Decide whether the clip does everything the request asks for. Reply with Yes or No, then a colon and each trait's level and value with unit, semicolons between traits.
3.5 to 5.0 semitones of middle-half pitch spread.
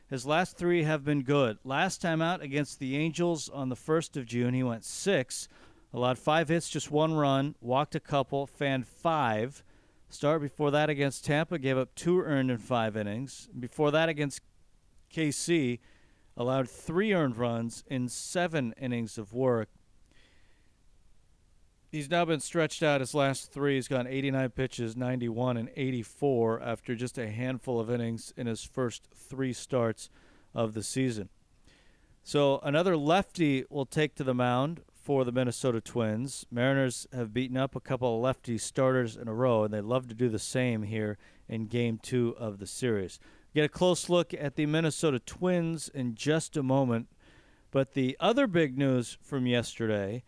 Yes: average, 4.1 semitones